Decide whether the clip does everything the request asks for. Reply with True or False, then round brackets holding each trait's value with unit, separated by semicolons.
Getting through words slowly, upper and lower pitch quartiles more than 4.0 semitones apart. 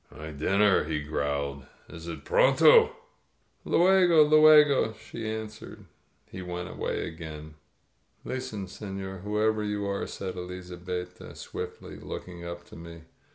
True (120 wpm; 4.5 semitones)